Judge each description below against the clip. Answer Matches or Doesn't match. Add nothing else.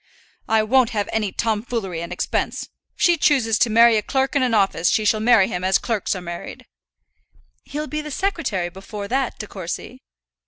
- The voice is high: Matches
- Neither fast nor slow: Matches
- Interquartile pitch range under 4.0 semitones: Doesn't match